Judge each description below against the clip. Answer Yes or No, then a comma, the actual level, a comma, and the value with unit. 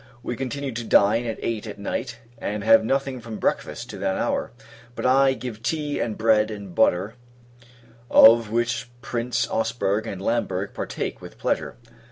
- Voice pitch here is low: Yes, low, 115 Hz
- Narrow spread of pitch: Yes, narrow, 2.3 semitones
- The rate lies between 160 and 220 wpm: Yes, average, 165 wpm